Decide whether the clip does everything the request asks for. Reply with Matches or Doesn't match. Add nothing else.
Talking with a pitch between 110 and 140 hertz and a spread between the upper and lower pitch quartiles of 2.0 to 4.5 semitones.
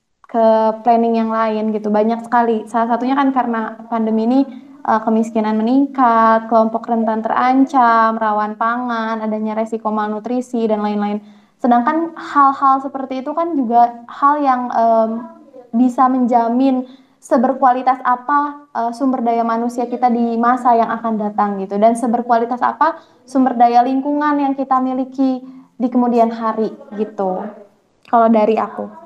Doesn't match